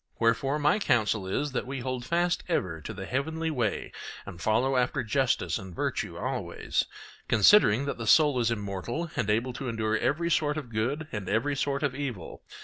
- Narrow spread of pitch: No, average, 4.9 semitones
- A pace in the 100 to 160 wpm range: No, average, 185 wpm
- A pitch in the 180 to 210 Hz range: No, low, 125 Hz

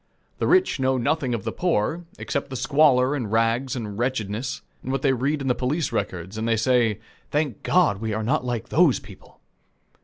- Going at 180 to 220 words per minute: Yes, average, 195 wpm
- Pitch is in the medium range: No, low, 125 Hz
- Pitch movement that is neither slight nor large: Yes, average, 3.9 semitones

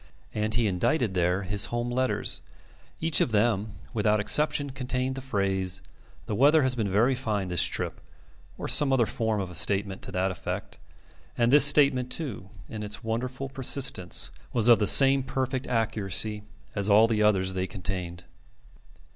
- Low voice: Yes, low, 110 Hz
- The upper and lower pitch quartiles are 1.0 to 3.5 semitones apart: No, average, 5.0 semitones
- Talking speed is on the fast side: No, average, 165 wpm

